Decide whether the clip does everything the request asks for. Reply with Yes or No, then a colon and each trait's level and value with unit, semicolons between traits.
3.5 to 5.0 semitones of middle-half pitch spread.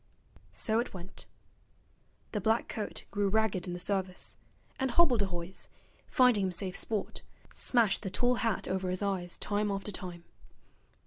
No: average, 3.1 semitones